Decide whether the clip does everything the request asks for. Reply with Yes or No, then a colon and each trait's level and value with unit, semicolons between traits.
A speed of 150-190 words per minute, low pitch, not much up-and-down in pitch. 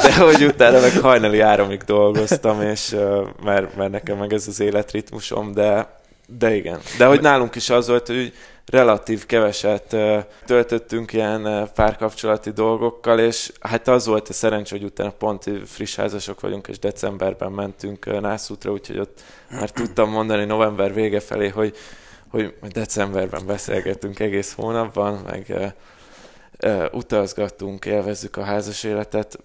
No: average, 140 wpm; low, 105 Hz; narrow, 1.6 semitones